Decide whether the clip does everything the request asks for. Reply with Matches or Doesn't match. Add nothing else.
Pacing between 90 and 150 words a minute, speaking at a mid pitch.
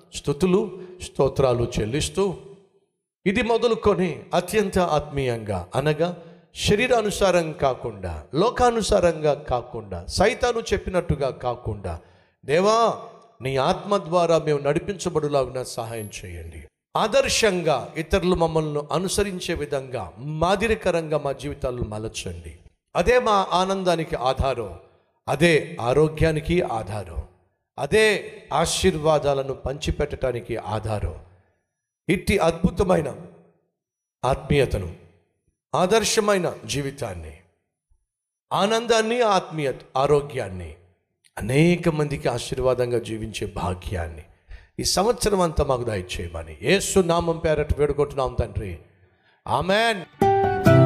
Doesn't match